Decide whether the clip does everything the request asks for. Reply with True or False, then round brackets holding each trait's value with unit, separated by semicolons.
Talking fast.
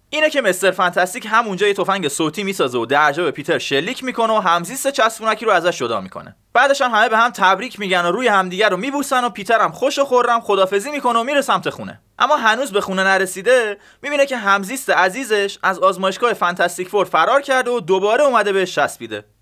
True (205 wpm)